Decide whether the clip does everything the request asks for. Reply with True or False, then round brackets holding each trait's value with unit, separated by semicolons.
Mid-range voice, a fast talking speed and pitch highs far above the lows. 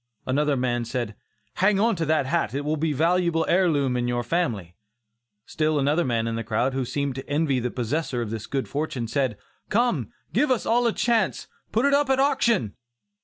True (145 Hz; 210 wpm; 6.6 semitones)